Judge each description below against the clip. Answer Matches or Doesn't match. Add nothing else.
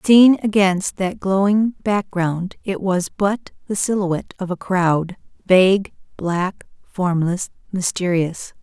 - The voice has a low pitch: Doesn't match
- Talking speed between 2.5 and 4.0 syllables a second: Matches